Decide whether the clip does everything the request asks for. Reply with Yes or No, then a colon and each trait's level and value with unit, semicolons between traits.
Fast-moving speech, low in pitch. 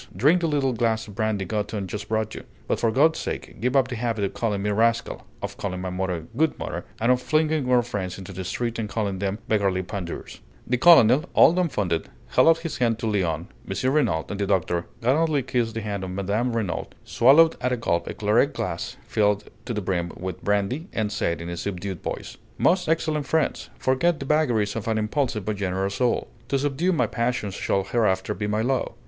Yes: fast, 215 wpm; low, 110 Hz